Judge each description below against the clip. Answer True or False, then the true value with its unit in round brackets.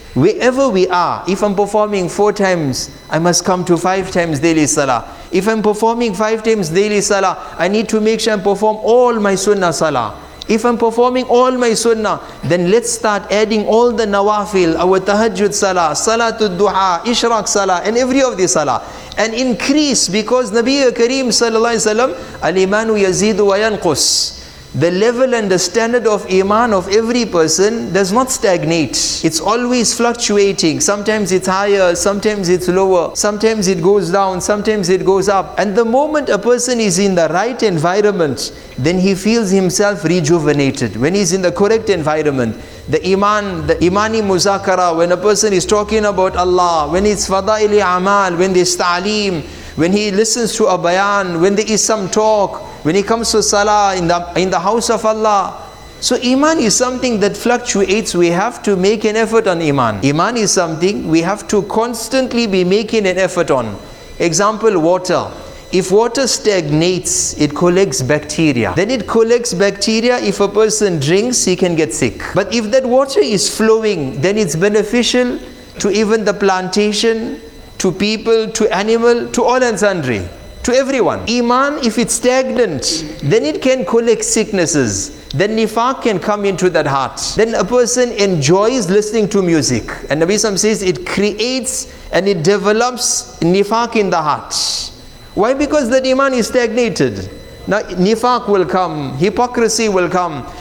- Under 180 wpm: True (170 wpm)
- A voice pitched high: True (205 Hz)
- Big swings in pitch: False (3.9 semitones)